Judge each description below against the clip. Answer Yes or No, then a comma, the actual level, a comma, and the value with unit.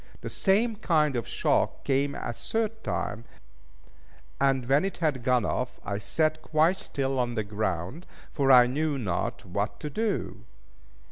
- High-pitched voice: No, low, 135 Hz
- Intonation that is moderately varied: Yes, average, 4.9 semitones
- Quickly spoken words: No, average, 155 wpm